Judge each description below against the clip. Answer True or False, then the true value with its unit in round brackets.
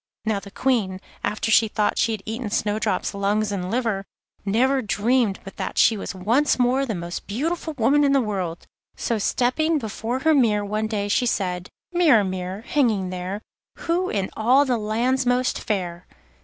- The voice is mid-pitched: False (220 Hz)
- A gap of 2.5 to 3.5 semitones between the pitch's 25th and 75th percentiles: False (4.2 semitones)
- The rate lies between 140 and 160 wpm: False (175 wpm)